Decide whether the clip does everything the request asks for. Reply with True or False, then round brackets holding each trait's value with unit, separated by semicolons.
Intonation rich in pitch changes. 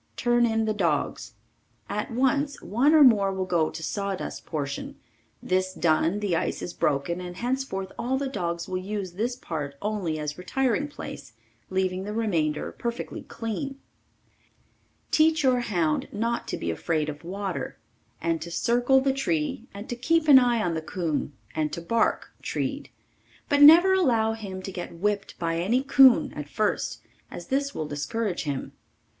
True (6.3 semitones)